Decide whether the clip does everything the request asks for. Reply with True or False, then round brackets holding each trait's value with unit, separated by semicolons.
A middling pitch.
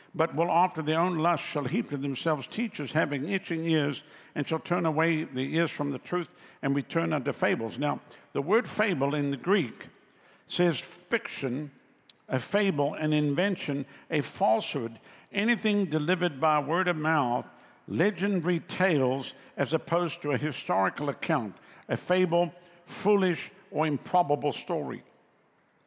True (160 Hz)